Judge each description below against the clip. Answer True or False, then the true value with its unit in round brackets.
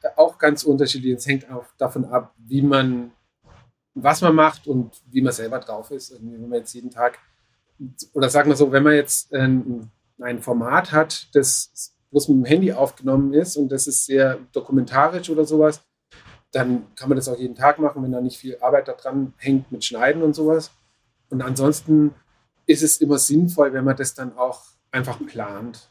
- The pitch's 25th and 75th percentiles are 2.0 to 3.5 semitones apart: True (2.8 semitones)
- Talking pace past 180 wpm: True (190 wpm)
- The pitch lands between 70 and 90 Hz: False (135 Hz)